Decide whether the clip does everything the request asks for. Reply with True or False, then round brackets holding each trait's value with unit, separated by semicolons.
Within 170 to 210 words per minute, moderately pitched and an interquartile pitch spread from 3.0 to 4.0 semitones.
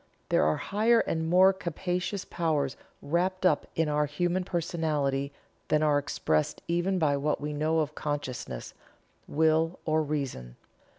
False (140 wpm; 155 Hz; 3.4 semitones)